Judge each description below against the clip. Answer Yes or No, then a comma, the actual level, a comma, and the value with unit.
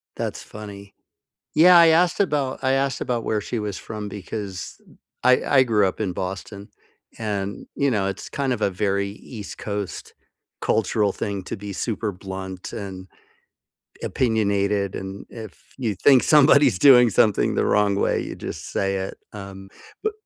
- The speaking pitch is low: Yes, low, 105 Hz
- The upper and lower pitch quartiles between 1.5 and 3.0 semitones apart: No, average, 4.2 semitones